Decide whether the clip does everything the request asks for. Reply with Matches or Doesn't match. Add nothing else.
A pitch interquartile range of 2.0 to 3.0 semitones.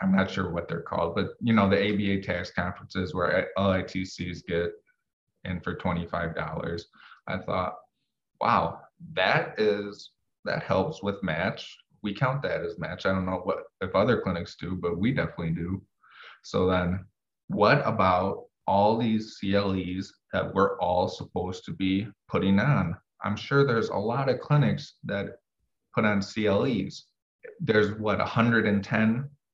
Matches